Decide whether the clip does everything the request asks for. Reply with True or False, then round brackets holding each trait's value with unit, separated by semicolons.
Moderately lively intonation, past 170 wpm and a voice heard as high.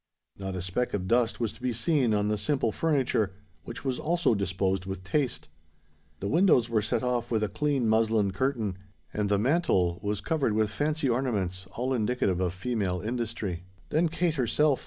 False (4.9 semitones; 180 wpm; 115 Hz)